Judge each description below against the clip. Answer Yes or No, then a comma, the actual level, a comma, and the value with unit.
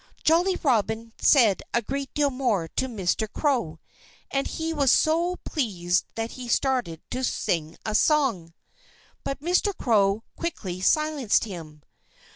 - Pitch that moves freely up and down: Yes, wide, 6.8 semitones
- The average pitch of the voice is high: Yes, high, 240 Hz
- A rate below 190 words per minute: Yes, slow, 135 wpm